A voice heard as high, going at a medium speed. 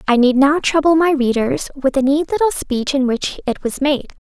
No: very high, 280 Hz; fast, 225 wpm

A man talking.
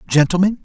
Yes: male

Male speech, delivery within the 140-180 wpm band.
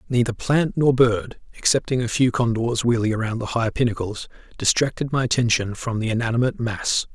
Yes: male; average, 170 wpm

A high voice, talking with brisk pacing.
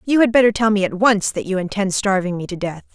Yes: high, 205 Hz; fast, 285 wpm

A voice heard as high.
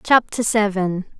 Yes: high, 205 Hz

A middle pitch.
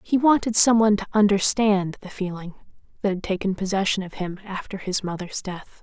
No: high, 195 Hz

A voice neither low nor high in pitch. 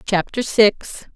No: high, 205 Hz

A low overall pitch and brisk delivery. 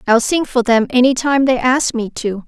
No: high, 245 Hz; fast, 245 wpm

